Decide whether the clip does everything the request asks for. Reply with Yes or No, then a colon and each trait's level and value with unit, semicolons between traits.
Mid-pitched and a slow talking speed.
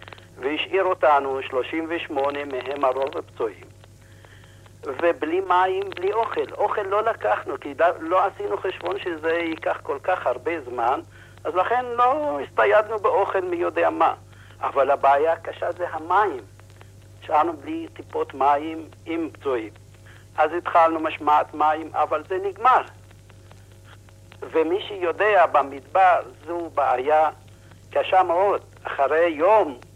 No: medium, 160 Hz; average, 115 wpm